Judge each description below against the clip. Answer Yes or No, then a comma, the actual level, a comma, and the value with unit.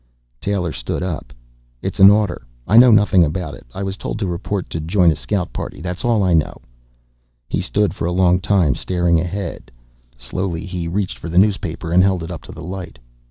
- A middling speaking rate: No, fast, 210 wpm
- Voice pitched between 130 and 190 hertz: No, very low, 90 Hz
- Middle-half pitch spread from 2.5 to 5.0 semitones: Yes, average, 2.8 semitones